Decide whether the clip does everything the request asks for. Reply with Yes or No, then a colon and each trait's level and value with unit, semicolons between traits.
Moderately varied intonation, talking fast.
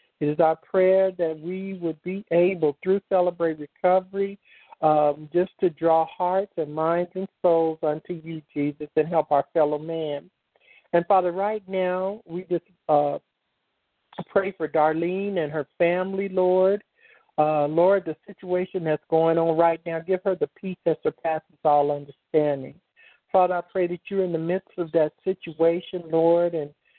No: average, 3.0 semitones; average, 160 wpm